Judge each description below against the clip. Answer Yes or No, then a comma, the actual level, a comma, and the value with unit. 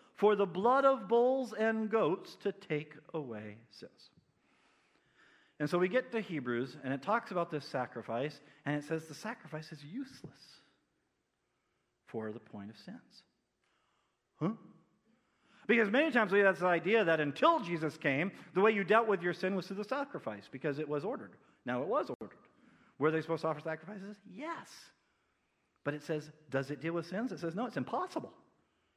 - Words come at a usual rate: Yes, average, 180 wpm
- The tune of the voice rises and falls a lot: Yes, wide, 6.5 semitones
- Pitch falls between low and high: Yes, medium, 175 Hz